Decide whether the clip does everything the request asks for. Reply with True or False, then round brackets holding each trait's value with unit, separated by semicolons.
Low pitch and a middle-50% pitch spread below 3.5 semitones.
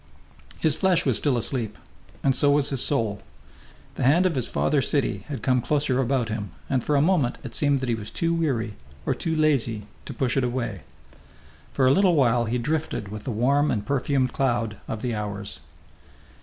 False (130 Hz; 4.1 semitones)